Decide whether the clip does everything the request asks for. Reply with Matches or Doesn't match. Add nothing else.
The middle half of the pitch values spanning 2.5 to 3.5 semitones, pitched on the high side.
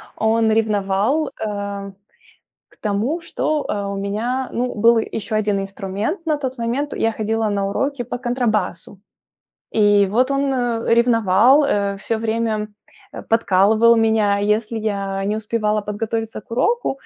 Matches